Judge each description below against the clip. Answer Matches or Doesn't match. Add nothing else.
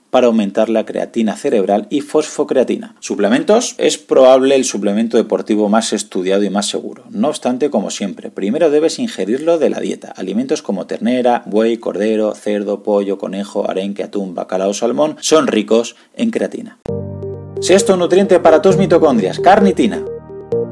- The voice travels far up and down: Matches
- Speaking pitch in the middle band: Doesn't match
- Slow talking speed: Doesn't match